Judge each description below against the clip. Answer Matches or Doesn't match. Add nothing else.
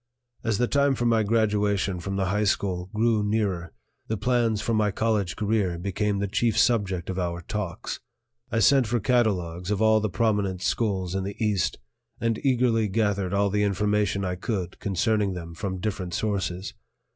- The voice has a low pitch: Matches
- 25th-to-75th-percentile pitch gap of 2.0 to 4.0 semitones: Matches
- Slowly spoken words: Doesn't match